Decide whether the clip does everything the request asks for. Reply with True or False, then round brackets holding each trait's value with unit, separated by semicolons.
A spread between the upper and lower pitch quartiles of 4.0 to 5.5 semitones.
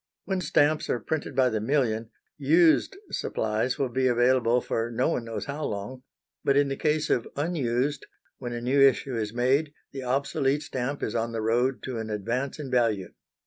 False (3.4 semitones)